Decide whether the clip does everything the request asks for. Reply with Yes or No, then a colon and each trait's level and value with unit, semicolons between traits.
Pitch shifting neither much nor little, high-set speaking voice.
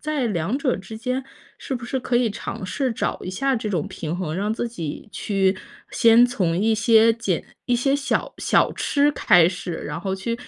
Yes: average, 4.8 semitones; high, 220 Hz